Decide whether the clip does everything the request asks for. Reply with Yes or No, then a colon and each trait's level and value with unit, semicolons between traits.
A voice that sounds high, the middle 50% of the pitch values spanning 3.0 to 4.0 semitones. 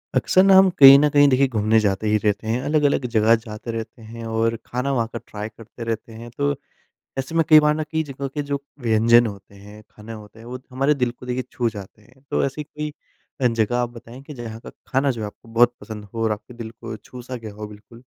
No: low, 115 Hz; average, 3.4 semitones